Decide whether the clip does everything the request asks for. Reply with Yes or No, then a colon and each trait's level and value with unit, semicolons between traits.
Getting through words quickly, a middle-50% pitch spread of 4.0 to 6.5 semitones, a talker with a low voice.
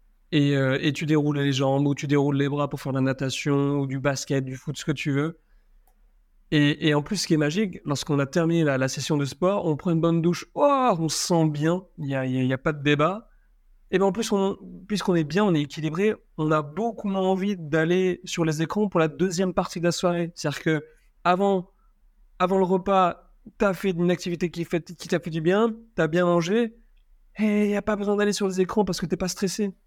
No: fast, 250 wpm; average, 4.6 semitones; medium, 175 Hz